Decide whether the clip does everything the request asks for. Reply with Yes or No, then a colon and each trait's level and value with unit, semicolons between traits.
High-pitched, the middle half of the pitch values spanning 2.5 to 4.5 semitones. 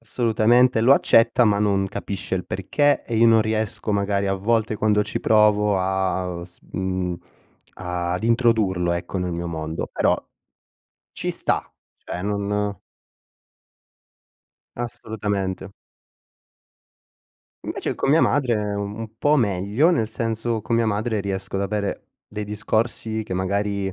No: low, 105 Hz; average, 2.8 semitones